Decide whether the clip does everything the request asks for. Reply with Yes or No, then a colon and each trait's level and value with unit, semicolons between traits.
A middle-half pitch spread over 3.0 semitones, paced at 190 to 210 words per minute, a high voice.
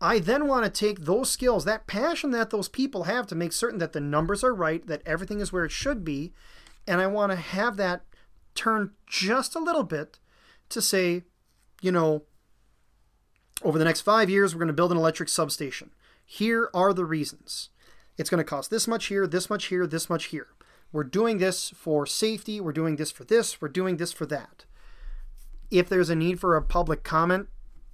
No: average, 5.0 semitones; fast, 205 wpm; medium, 180 Hz